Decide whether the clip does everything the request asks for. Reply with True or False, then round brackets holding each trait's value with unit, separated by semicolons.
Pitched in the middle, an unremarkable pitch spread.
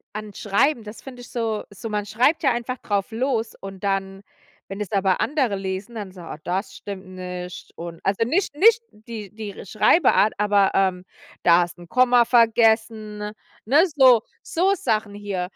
False (210 Hz; 3.6 semitones)